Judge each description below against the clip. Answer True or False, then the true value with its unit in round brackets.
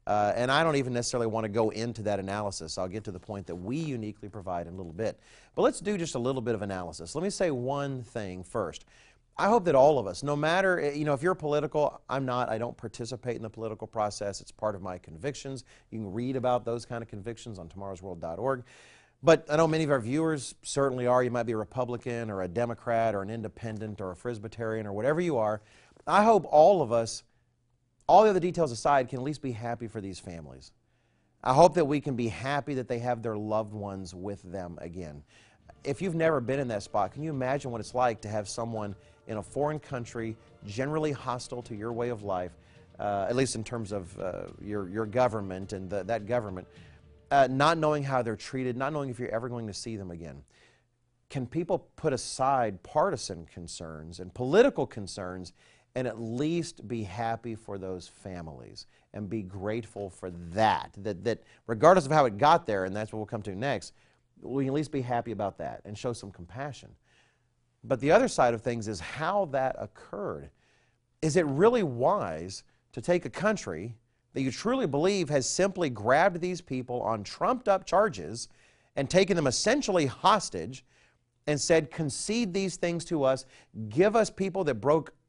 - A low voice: True (120 Hz)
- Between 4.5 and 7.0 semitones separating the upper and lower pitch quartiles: True (5.1 semitones)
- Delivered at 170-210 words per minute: True (205 wpm)